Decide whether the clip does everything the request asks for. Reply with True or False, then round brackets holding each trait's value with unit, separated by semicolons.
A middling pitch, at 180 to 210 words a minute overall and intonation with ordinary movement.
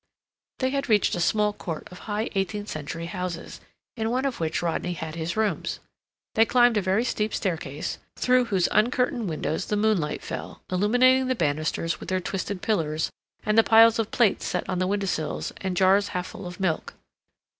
False (195 Hz; 190 wpm; 4.5 semitones)